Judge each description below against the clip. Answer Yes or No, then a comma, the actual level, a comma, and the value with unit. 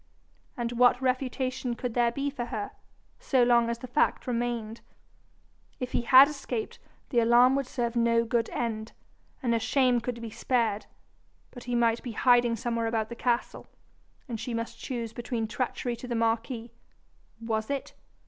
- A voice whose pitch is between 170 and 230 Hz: No, high, 240 Hz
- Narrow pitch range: Yes, narrow, 1.5 semitones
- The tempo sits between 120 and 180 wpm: Yes, average, 165 wpm